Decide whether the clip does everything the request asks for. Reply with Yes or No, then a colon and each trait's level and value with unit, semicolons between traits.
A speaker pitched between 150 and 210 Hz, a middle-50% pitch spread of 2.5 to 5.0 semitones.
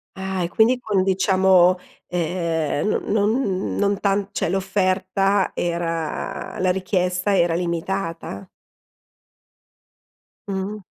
No: medium, 185 Hz; narrow, 2.1 semitones